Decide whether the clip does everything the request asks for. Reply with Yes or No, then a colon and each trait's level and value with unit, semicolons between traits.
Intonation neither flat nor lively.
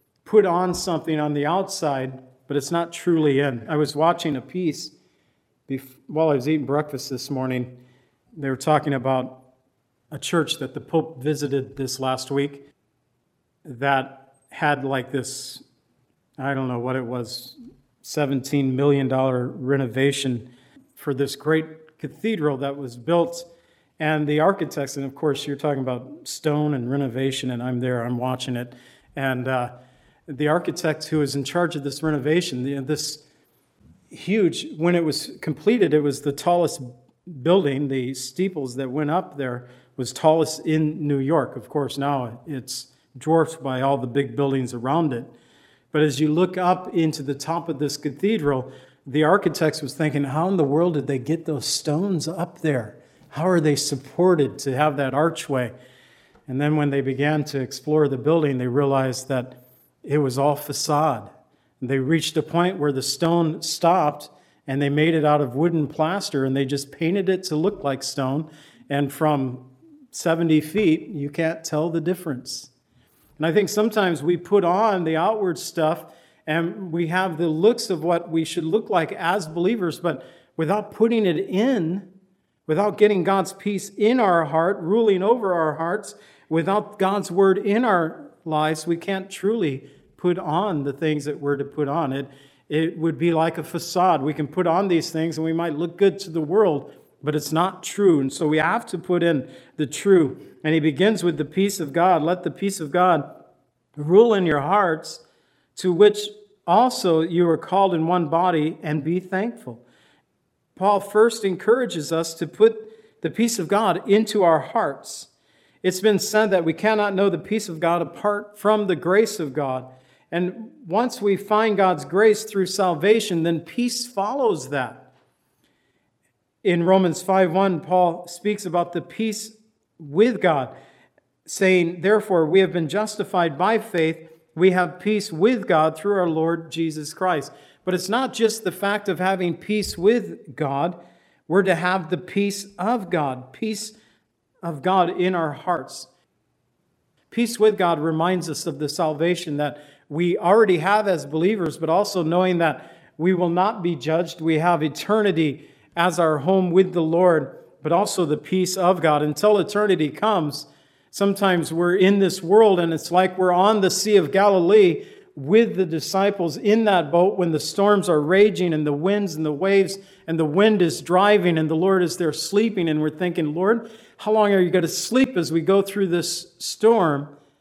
Yes: average, 4.7 semitones